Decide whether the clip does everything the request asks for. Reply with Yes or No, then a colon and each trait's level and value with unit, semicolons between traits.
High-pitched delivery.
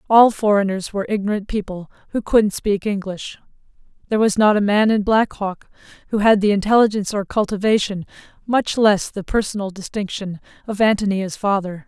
Yes: high, 205 Hz